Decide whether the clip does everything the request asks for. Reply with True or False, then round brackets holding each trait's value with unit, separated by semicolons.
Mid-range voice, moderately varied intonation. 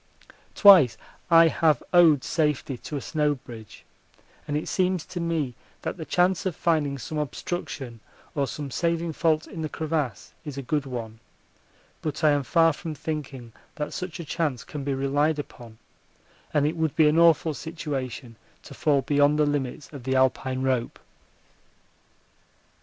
True (150 Hz; 3.3 semitones)